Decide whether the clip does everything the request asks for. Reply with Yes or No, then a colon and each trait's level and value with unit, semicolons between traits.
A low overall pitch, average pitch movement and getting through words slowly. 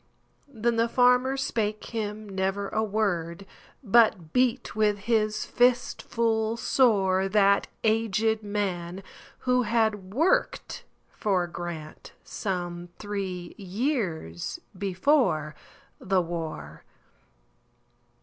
No: high, 205 Hz; average, 3.8 semitones; slow, 85 wpm